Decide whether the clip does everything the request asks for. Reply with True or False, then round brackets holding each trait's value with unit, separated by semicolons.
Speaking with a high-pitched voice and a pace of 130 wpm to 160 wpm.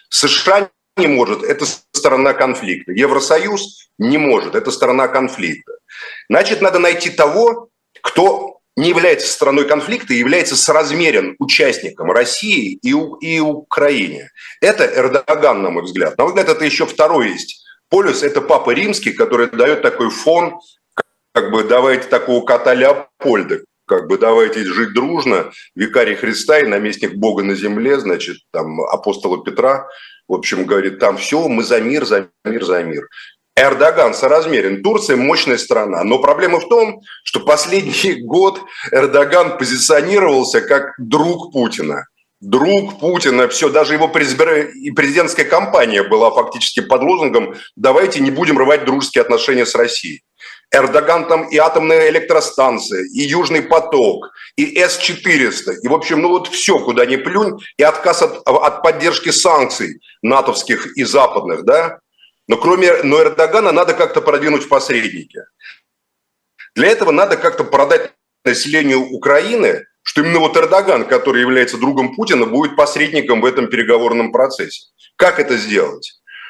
True (265 Hz; 140 wpm)